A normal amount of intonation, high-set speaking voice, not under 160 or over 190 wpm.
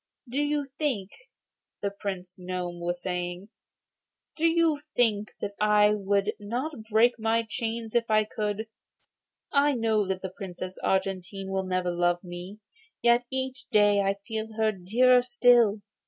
No: average, 3.9 semitones; high, 210 Hz; average, 145 wpm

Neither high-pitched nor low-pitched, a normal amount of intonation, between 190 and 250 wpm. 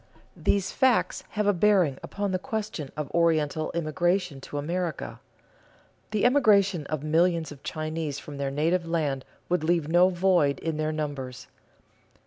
No: medium, 165 Hz; average, 3.7 semitones; average, 145 wpm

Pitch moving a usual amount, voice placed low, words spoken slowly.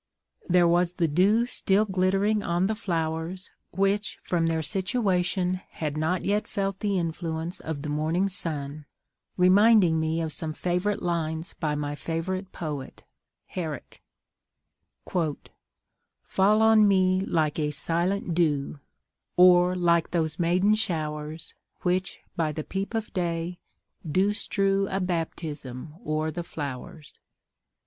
No: average, 3.3 semitones; medium, 175 Hz; slow, 125 wpm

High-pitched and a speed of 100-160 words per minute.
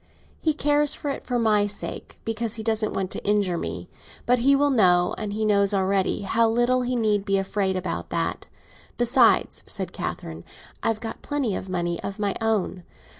No: high, 215 Hz; average, 175 wpm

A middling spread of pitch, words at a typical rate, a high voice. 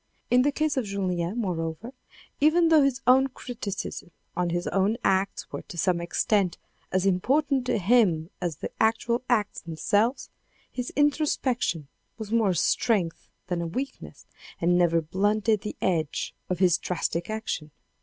No: wide, 5.9 semitones; average, 155 wpm; high, 200 Hz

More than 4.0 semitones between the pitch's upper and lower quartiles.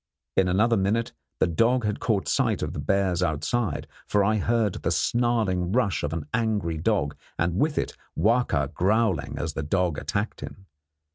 Yes: average, 5.2 semitones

